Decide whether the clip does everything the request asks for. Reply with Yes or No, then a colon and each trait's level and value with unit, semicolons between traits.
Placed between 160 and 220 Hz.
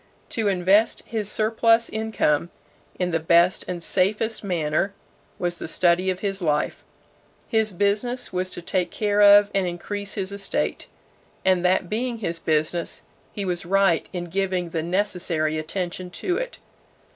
Yes: medium, 185 Hz